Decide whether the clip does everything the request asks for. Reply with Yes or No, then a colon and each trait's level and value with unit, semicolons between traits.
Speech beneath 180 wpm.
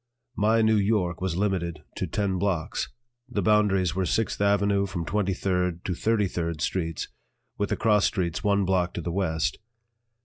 Yes: average, 170 wpm